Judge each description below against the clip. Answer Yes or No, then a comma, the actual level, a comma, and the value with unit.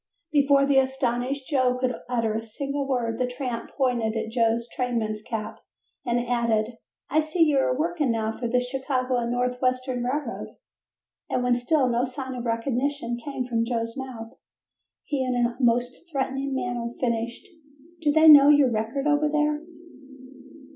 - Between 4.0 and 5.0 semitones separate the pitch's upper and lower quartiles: No, average, 2.8 semitones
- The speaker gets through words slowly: No, average, 160 wpm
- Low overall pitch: No, very high, 250 Hz